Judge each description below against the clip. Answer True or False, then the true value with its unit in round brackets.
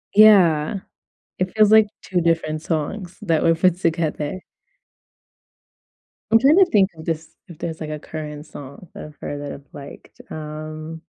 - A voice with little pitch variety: False (3.2 semitones)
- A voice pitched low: False (160 Hz)